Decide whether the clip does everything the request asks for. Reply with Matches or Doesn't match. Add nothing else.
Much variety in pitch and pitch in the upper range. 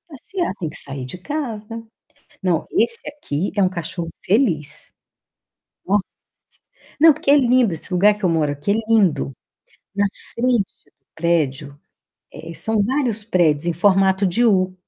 Matches